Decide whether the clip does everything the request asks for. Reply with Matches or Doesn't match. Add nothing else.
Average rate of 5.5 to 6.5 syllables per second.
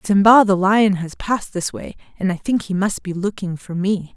Doesn't match